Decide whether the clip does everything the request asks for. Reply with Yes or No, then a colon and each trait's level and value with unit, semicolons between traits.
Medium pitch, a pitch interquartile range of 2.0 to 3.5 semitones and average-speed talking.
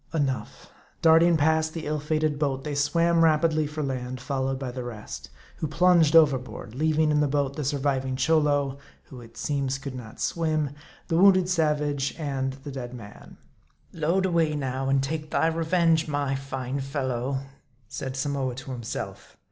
Yes: medium, 145 Hz; average, 3.0 semitones; average, 165 wpm